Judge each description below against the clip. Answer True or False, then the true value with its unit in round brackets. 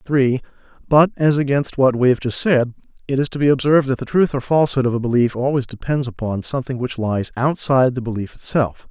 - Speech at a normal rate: False (215 wpm)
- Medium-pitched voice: False (130 Hz)